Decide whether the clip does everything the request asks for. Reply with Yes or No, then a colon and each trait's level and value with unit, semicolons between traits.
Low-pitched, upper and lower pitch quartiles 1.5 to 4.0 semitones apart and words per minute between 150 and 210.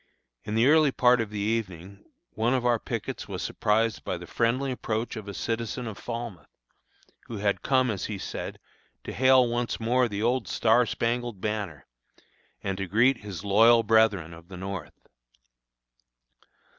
Yes: low, 110 Hz; average, 3.2 semitones; average, 165 wpm